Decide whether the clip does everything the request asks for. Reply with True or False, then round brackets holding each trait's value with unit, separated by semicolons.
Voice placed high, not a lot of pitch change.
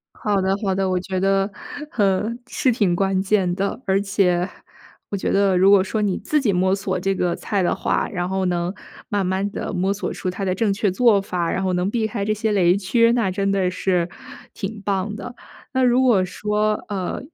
True (195 Hz; 2.0 semitones)